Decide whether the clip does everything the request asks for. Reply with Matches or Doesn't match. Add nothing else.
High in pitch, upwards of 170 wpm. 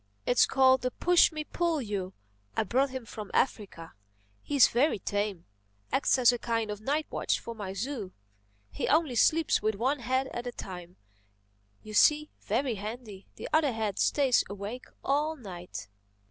Doesn't match